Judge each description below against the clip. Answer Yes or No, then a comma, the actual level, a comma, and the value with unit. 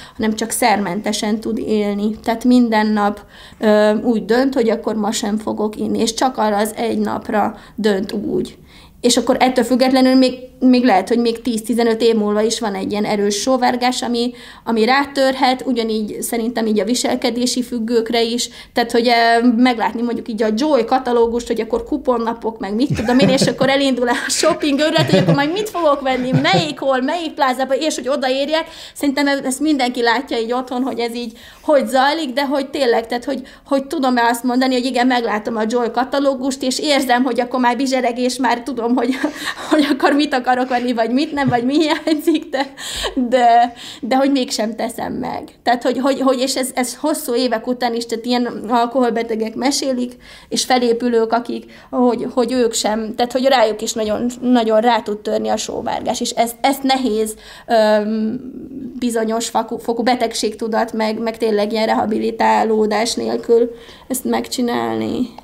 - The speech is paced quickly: Yes, fast, 175 wpm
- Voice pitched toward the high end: Yes, high, 245 Hz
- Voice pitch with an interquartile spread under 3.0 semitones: Yes, narrow, 2.6 semitones